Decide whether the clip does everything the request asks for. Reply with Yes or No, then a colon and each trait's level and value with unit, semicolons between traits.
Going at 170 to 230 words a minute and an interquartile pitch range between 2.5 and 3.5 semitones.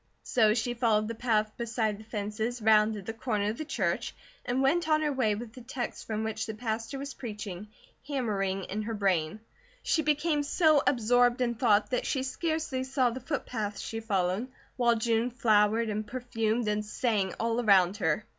Yes: average, 185 wpm; average, 3.1 semitones